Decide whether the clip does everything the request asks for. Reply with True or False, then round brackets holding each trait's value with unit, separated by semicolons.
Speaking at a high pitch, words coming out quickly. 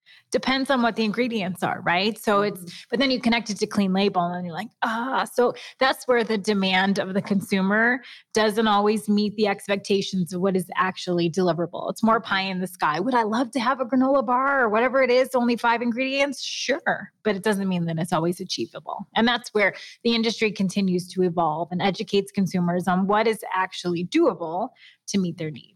True (205 Hz; 210 wpm)